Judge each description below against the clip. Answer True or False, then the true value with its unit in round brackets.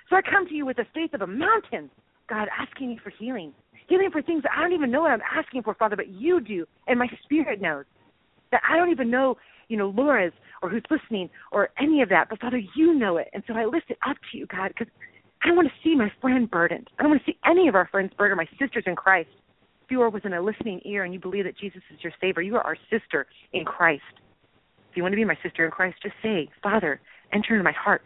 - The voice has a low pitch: False (225 Hz)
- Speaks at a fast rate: True (270 wpm)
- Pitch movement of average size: False (7.4 semitones)